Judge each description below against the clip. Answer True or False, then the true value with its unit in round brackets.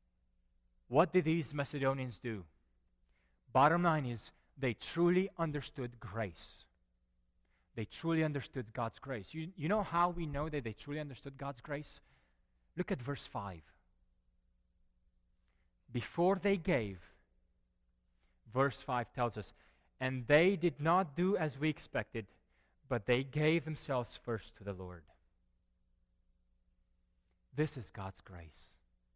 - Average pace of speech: False (125 wpm)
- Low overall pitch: True (110 Hz)